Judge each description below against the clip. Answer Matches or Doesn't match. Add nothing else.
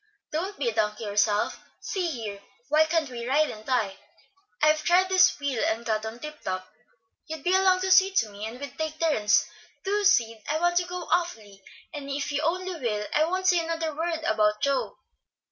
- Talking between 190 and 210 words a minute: Matches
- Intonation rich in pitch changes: Matches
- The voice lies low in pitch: Doesn't match